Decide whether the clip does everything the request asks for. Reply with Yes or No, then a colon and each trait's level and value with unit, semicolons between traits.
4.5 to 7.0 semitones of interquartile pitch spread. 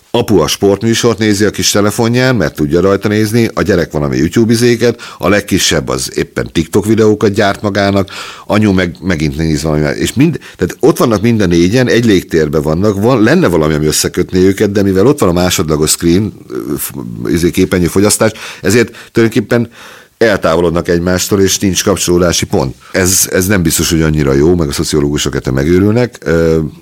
Yes: average, 4.8 semitones